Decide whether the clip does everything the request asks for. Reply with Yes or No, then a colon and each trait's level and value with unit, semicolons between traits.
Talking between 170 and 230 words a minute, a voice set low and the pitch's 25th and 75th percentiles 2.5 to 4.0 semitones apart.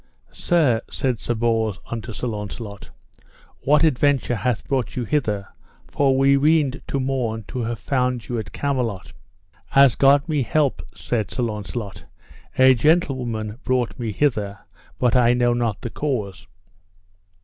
No: average, 145 wpm; low, 120 Hz; average, 3.7 semitones